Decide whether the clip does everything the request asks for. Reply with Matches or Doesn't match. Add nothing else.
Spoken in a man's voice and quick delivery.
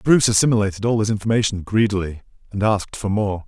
Doesn't match